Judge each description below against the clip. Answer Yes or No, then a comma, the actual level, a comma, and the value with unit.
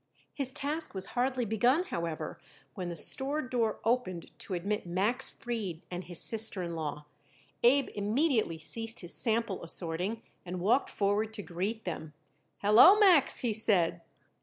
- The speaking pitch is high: Yes, high, 215 Hz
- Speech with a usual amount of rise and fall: No, wide, 5.7 semitones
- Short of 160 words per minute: Yes, average, 150 wpm